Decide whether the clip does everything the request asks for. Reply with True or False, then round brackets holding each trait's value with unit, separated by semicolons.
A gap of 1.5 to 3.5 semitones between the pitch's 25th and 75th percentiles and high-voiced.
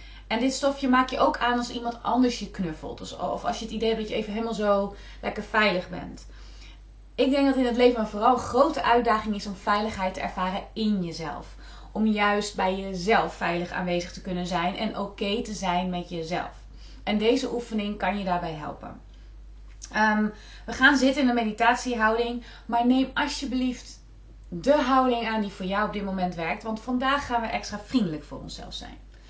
False (4.2 semitones; 215 Hz)